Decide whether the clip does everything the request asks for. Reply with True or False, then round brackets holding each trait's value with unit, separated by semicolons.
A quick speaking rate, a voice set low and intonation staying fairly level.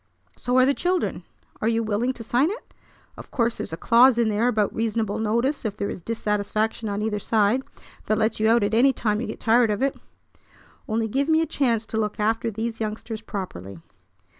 False (210 wpm; 225 Hz; 2.3 semitones)